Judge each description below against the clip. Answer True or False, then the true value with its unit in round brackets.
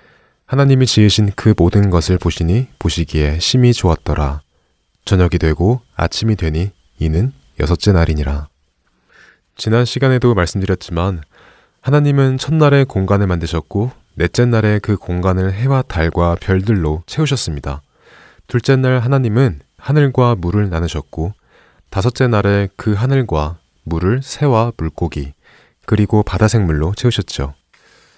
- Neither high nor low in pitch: False (95 Hz)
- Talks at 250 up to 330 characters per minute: True (285 characters per minute)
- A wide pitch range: True (6.6 semitones)